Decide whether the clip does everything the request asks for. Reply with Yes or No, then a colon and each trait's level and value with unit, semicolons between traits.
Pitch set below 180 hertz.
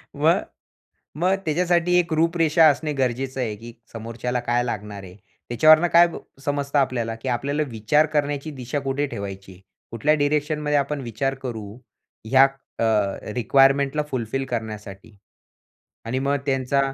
Yes: low, 135 Hz